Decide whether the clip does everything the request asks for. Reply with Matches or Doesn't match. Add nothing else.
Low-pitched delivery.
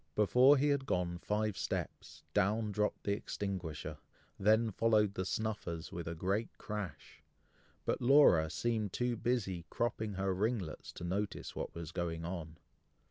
Matches